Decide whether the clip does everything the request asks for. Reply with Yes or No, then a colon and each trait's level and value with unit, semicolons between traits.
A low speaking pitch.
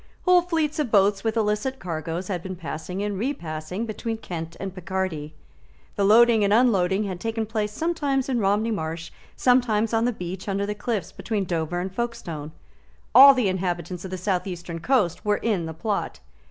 No: high, 200 Hz